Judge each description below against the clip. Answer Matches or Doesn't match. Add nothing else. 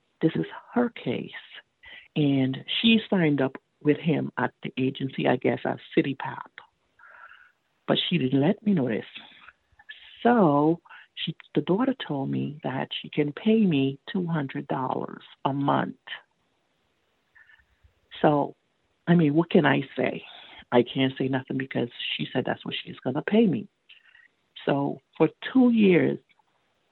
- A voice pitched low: Doesn't match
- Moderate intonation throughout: Doesn't match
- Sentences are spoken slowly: Doesn't match